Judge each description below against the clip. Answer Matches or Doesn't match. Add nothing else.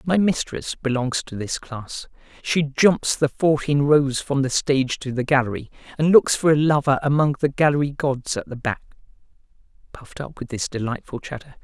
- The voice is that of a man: Matches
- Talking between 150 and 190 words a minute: Matches